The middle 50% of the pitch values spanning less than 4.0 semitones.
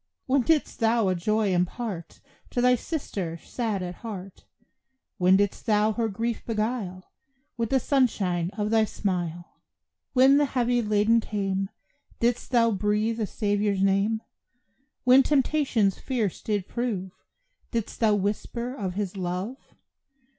Yes: average, 3.6 semitones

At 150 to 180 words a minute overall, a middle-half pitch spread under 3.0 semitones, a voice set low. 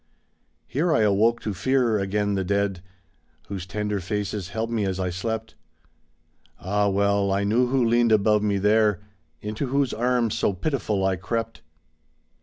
Yes: average, 155 wpm; narrow, 2.5 semitones; low, 105 Hz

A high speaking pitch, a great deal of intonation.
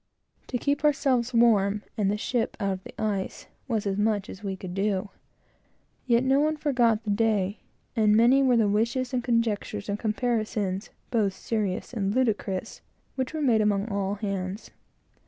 No: high, 215 Hz; average, 3.3 semitones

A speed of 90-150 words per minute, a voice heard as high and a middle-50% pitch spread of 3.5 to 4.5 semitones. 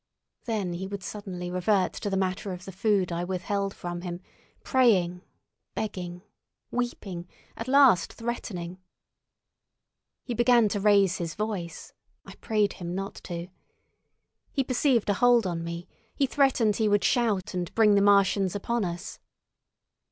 Yes: average, 140 wpm; high, 200 Hz; average, 3.8 semitones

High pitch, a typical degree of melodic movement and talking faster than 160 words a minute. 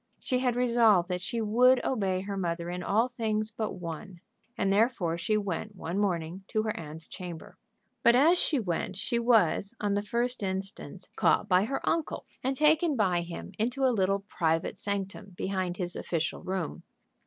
Yes: high, 200 Hz; average, 4.6 semitones; average, 175 wpm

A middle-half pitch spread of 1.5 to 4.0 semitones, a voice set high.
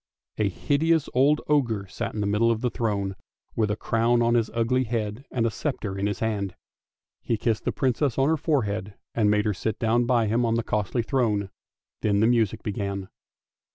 No: average, 2.8 semitones; low, 115 Hz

